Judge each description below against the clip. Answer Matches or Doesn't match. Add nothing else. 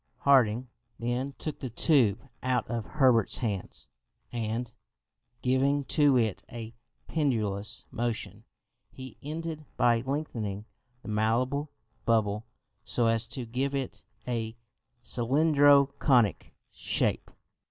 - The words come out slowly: Matches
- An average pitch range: Matches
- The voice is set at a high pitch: Doesn't match